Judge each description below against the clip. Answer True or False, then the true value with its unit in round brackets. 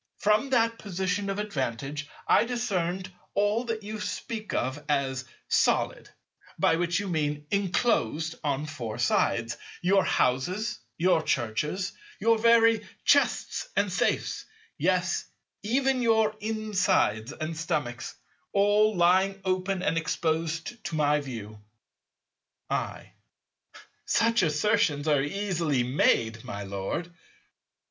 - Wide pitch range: True (6.3 semitones)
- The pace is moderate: False (115 wpm)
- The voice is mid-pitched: True (175 Hz)